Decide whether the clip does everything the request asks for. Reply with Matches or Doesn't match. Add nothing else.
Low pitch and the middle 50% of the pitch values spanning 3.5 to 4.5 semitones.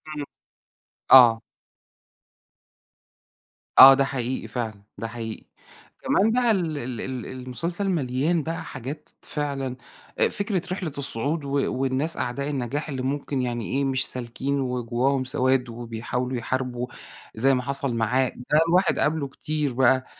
Doesn't match